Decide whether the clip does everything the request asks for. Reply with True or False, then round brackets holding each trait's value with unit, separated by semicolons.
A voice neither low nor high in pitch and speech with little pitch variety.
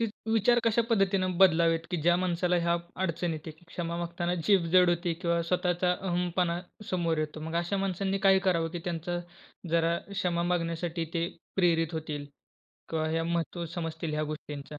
True (170 Hz; 1.6 semitones)